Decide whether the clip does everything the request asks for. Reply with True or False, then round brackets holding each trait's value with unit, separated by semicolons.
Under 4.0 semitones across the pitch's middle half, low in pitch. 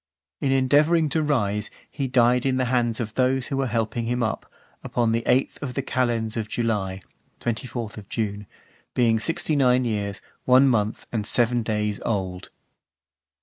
True (3.0 semitones; 120 Hz)